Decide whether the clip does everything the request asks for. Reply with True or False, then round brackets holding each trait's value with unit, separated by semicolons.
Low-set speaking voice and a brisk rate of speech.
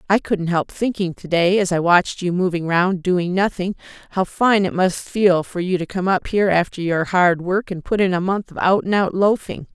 False (185 Hz; 240 wpm)